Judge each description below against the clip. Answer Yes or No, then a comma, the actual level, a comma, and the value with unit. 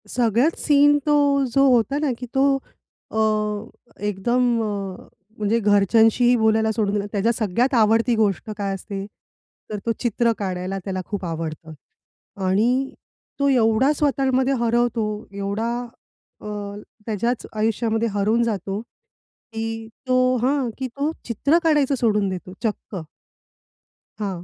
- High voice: Yes, high, 225 Hz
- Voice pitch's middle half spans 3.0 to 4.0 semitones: Yes, average, 3.7 semitones